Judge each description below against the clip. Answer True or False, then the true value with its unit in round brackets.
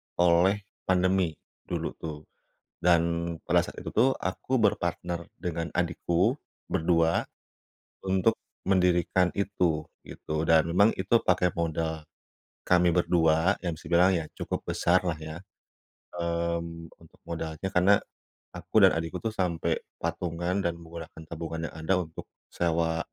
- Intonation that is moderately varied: False (2.0 semitones)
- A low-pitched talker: True (85 Hz)